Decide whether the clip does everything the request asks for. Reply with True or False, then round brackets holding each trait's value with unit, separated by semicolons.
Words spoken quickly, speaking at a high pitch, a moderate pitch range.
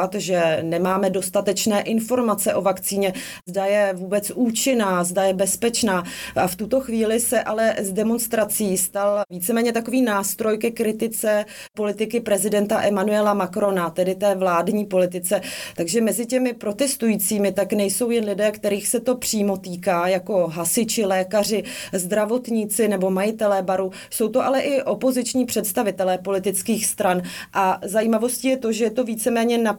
False (145 wpm; 210 Hz; 3.0 semitones)